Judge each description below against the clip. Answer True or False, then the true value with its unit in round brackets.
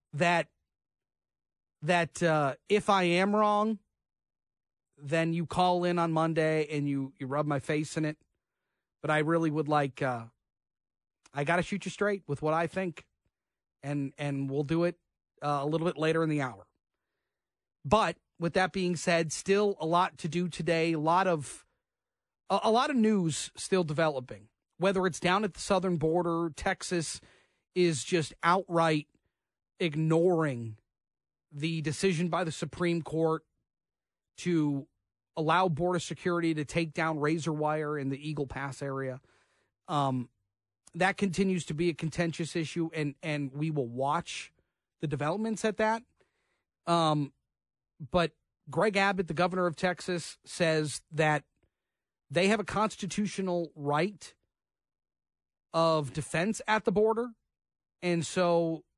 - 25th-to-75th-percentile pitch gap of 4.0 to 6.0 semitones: False (3.5 semitones)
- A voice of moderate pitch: True (165 Hz)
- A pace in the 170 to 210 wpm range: False (145 wpm)